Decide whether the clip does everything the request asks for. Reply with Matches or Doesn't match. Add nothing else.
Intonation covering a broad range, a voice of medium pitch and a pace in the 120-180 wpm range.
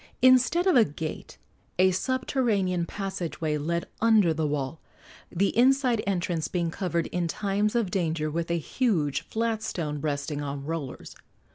Matches